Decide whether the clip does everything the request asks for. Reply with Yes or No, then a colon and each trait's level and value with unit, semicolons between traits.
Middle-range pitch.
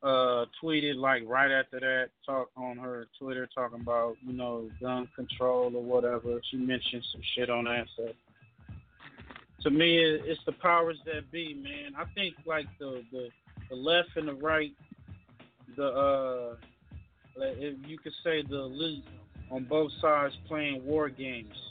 No: low, 130 Hz